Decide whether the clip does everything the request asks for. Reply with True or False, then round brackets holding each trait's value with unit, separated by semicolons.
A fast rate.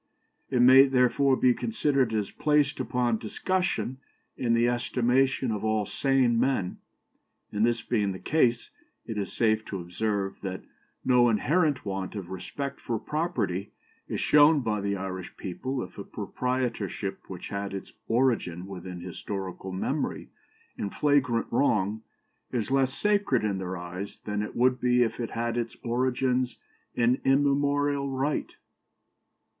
False (145 wpm)